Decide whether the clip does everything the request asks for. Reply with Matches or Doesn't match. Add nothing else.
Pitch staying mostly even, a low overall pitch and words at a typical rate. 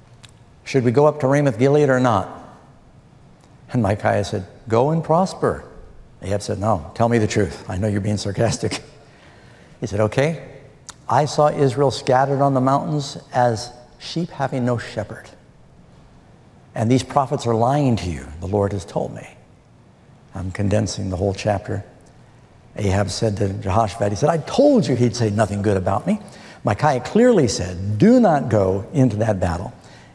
Doesn't match